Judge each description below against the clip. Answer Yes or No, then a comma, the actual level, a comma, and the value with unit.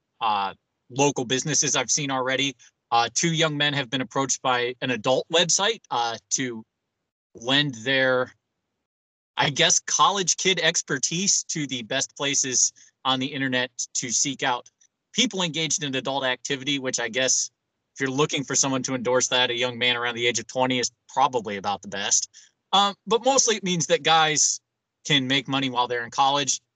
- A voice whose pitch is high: No, low, 130 Hz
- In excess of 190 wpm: No, average, 175 wpm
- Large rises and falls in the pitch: No, average, 3.2 semitones